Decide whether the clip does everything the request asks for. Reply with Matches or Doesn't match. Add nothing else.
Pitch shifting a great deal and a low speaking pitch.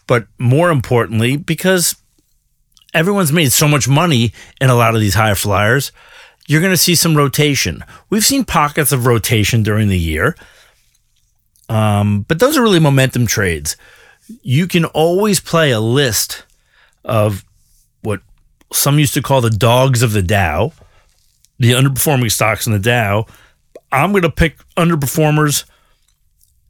Matches